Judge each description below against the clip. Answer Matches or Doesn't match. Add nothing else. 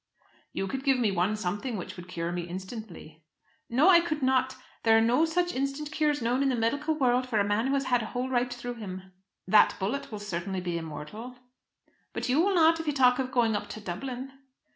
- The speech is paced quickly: Matches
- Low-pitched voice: Doesn't match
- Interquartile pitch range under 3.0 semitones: Doesn't match